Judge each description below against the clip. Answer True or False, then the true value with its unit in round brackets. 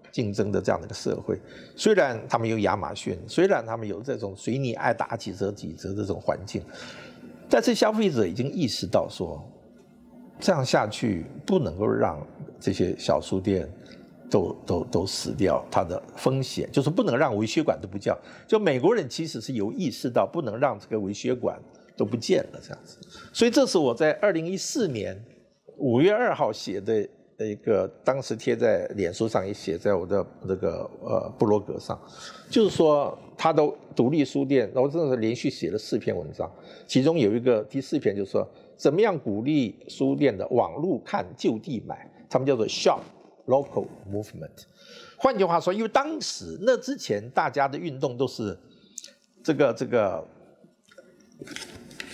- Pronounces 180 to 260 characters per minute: False (270 characters per minute)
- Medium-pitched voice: True (145 Hz)